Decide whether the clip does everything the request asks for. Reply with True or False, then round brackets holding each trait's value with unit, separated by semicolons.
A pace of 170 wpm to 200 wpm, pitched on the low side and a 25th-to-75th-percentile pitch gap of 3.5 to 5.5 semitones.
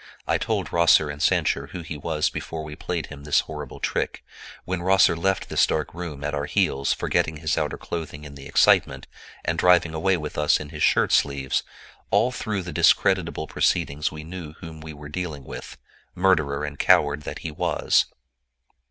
False (180 wpm; 80 Hz; 2.8 semitones)